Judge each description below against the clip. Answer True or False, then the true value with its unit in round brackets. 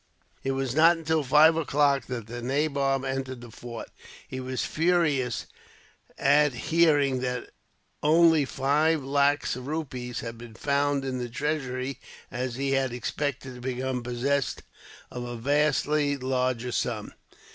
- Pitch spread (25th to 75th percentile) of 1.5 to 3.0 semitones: True (2.7 semitones)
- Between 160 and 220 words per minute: False (140 wpm)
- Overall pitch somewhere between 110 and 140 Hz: True (135 Hz)